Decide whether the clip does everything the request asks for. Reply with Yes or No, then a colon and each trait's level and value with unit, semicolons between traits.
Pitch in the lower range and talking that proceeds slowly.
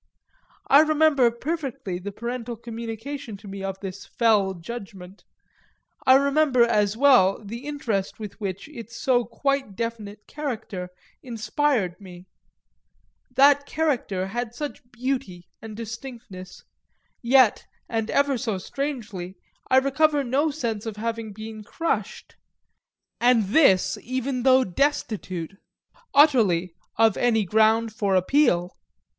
No: high, 230 Hz; slow, 120 wpm